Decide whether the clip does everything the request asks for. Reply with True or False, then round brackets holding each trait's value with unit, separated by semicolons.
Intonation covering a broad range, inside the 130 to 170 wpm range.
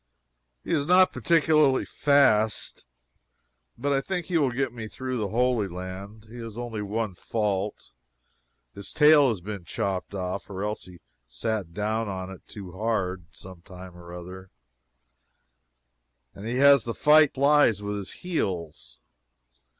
True (6.0 semitones; 155 wpm)